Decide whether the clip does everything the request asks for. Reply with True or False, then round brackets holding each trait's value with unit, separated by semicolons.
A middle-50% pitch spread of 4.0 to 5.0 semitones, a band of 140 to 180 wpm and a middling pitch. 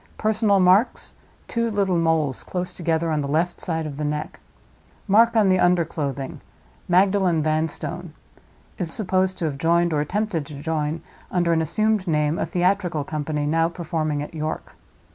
False (3.3 semitones; 155 wpm; 165 Hz)